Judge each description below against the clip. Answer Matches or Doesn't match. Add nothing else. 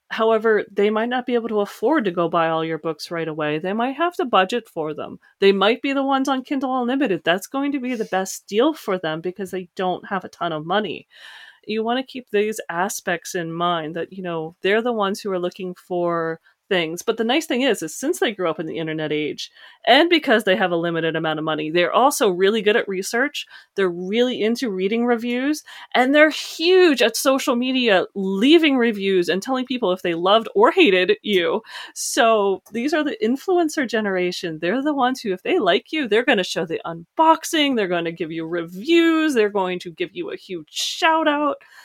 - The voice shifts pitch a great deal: Matches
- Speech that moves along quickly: Matches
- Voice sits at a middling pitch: Doesn't match